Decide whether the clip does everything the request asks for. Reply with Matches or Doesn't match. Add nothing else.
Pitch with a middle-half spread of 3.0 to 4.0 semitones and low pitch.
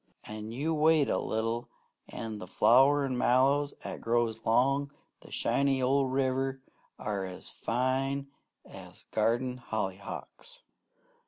Matches